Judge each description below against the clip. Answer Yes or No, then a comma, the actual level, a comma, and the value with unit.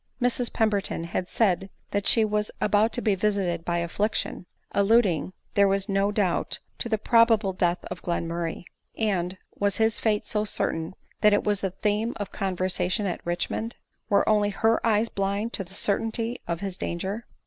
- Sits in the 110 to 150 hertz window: No, high, 200 Hz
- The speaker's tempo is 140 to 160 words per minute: No, average, 180 wpm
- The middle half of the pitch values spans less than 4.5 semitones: Yes, average, 2.9 semitones